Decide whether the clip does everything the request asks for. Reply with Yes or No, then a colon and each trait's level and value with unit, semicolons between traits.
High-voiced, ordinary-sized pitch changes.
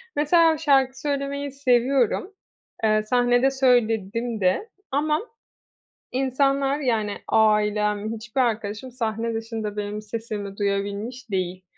Yes: high, 230 Hz; average, 4.2 semitones